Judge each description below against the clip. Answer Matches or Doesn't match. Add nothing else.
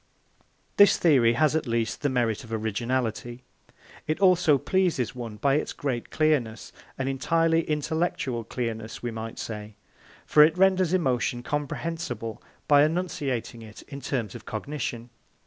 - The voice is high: Doesn't match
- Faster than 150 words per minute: Doesn't match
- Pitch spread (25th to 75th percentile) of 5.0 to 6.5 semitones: Matches